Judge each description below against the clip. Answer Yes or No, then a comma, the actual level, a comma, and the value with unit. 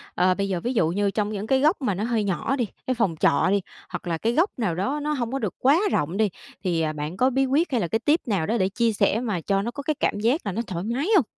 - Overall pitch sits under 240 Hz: Yes, high, 220 Hz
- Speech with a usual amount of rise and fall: No, wide, 5.7 semitones